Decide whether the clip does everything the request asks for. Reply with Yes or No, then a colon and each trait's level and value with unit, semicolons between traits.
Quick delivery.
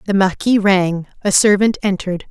No: average, 155 wpm